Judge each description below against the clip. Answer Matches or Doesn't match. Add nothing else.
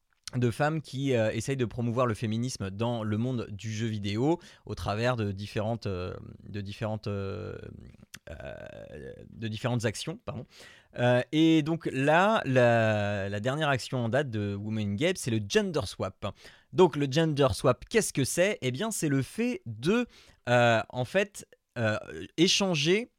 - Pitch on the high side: Doesn't match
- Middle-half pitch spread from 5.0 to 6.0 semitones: Matches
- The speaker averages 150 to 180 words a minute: Matches